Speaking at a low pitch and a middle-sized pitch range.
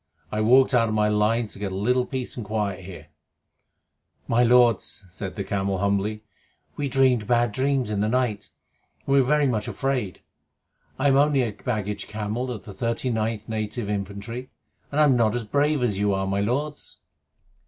Yes: low, 115 Hz; average, 3.6 semitones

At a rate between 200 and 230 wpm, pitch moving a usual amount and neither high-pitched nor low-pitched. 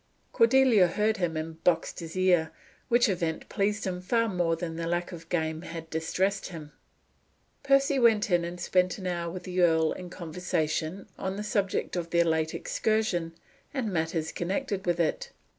No: average, 175 wpm; average, 3.3 semitones; medium, 175 Hz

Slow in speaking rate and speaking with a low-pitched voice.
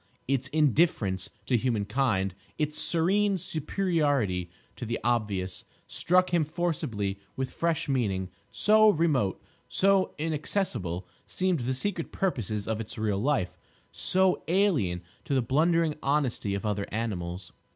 Yes: slow, 130 wpm; low, 130 Hz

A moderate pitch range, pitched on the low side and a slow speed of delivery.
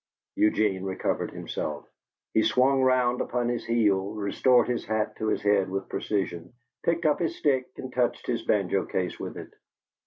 No: average, 4.2 semitones; low, 110 Hz; average, 165 wpm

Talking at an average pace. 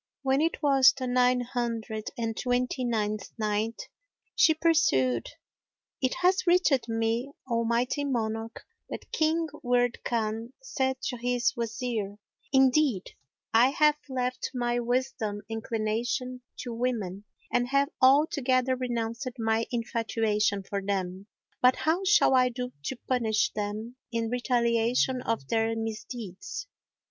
No: slow, 125 wpm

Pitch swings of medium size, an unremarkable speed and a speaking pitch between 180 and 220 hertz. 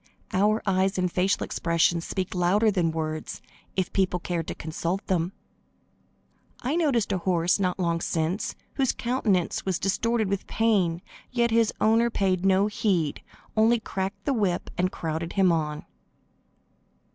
Yes: average, 3.8 semitones; average, 150 wpm; high, 190 Hz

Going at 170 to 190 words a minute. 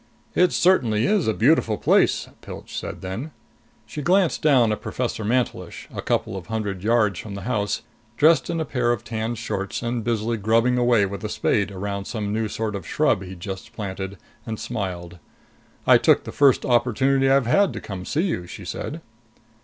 Yes: average, 185 wpm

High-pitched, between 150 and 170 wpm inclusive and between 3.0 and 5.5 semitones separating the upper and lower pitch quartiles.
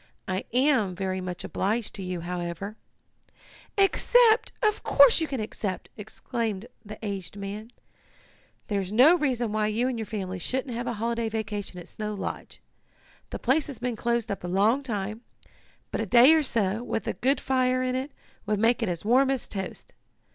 No: high, 225 Hz; average, 185 wpm; average, 4.3 semitones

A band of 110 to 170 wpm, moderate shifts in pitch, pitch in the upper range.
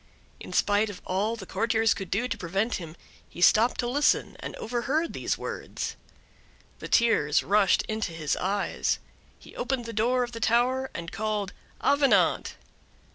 Yes: average, 160 wpm; average, 3.7 semitones; high, 220 Hz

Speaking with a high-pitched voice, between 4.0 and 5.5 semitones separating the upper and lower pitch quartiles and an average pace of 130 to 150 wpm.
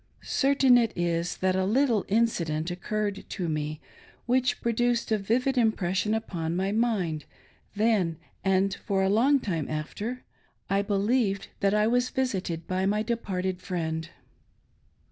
Yes: high, 200 Hz; average, 4.5 semitones; average, 145 wpm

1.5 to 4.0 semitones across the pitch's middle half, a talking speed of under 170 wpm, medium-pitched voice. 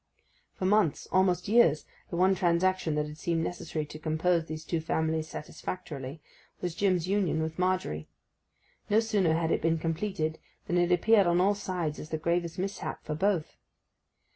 Yes: average, 2.9 semitones; average, 160 wpm; medium, 170 Hz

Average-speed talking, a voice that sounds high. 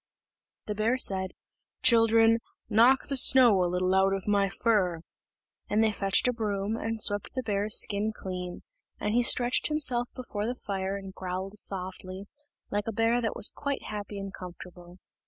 Yes: average, 170 wpm; high, 205 Hz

